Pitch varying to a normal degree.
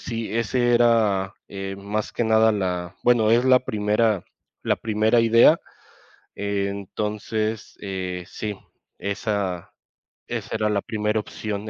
No: narrow, 2.2 semitones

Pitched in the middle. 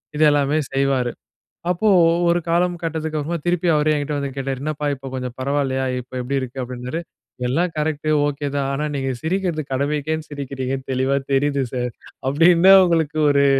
Yes: medium, 145 Hz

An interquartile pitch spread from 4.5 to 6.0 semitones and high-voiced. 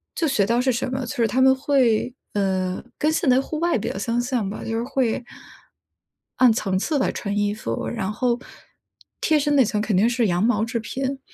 No: average, 4.1 semitones; high, 235 Hz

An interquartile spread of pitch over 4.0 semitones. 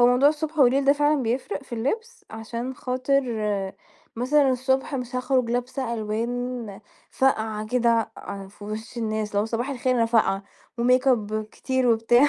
No: average, 2.9 semitones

